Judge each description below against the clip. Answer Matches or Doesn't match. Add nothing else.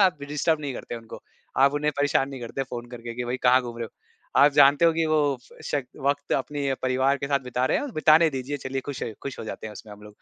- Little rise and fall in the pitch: Doesn't match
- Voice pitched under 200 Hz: Matches